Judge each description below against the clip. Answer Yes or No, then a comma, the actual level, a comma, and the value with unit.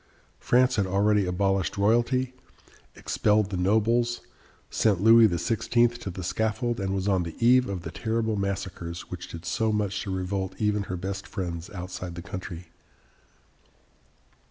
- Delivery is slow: No, average, 150 wpm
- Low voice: Yes, low, 100 Hz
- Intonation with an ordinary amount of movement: Yes, average, 3.4 semitones